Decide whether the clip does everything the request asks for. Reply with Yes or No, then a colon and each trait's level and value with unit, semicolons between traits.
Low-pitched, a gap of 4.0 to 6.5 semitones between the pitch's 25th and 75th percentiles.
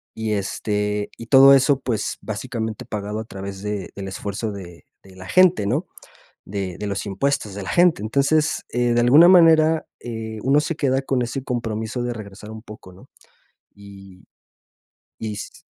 Yes: low, 110 Hz; average, 4.8 semitones